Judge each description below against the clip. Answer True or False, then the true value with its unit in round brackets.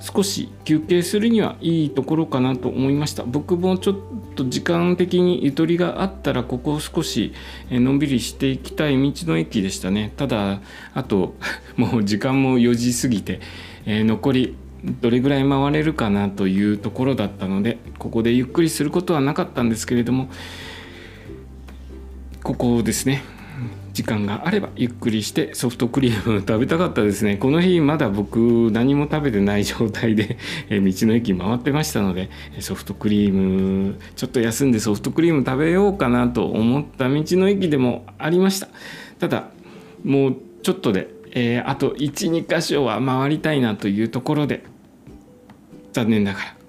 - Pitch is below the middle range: True (125 Hz)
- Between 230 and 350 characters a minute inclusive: True (330 characters per minute)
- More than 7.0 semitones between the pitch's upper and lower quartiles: False (5.8 semitones)